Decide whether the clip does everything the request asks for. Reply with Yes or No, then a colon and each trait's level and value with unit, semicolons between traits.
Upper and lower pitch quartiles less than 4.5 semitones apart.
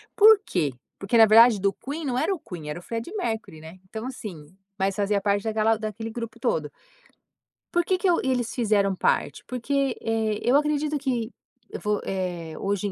No: average, 4.9 semitones